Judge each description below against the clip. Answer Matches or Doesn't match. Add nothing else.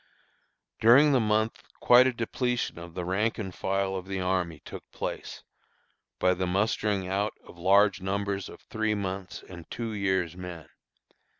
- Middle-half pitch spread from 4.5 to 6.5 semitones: Doesn't match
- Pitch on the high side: Doesn't match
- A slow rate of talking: Doesn't match